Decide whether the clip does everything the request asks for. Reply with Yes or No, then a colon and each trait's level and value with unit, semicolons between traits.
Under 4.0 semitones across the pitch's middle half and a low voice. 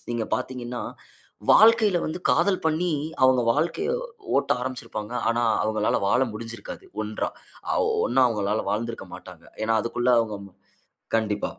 Yes: average, 3.5 semitones; low, 120 Hz